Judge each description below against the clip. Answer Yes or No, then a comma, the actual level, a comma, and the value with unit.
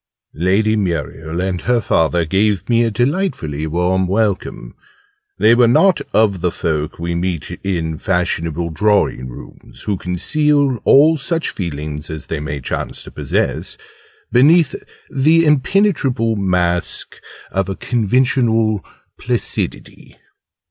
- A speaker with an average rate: No, slow, 120 wpm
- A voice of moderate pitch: No, very low, 95 Hz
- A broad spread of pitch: Yes, wide, 6.5 semitones